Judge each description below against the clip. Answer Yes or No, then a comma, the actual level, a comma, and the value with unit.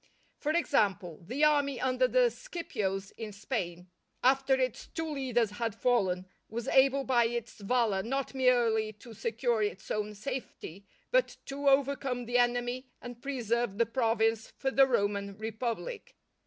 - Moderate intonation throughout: Yes, average, 3.9 semitones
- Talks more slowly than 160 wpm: Yes, average, 145 wpm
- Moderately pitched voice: No, high, 240 Hz